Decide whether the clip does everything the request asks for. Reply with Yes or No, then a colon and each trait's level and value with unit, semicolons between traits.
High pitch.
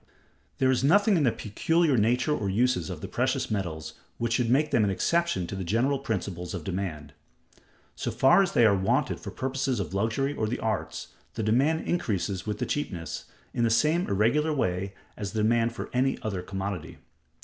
No: low, 110 Hz